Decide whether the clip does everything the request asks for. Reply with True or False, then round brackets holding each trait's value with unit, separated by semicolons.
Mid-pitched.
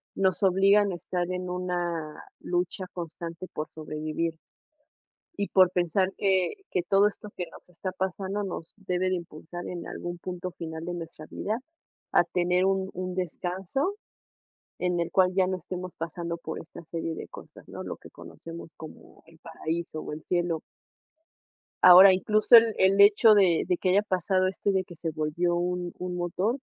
True (180 Hz)